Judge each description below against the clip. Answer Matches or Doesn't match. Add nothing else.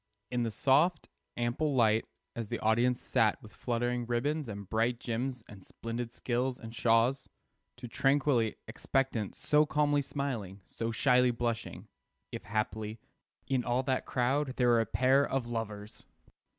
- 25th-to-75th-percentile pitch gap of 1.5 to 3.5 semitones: Matches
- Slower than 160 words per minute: Matches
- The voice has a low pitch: Matches